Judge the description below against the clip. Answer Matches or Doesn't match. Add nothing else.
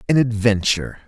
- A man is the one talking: Matches